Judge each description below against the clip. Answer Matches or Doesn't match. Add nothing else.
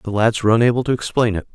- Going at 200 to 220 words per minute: Doesn't match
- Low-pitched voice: Matches